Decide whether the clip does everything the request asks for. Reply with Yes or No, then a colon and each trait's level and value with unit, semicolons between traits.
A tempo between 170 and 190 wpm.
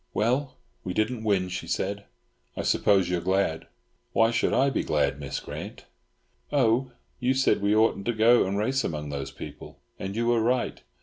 Yes: average, 185 wpm